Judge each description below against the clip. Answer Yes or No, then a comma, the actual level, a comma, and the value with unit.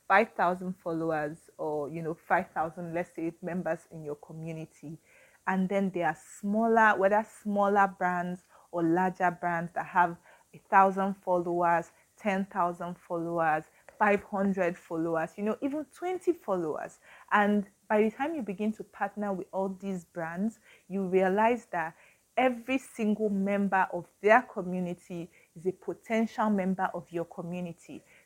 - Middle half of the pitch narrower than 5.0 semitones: Yes, average, 3.2 semitones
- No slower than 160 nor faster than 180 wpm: No, average, 145 wpm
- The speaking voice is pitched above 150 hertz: Yes, medium, 185 Hz